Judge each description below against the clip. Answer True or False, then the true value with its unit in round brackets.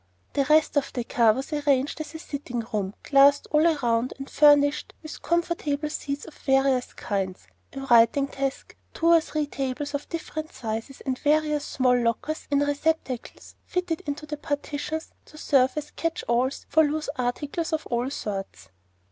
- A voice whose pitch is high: True (285 Hz)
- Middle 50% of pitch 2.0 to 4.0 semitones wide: True (3.2 semitones)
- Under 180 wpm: True (165 wpm)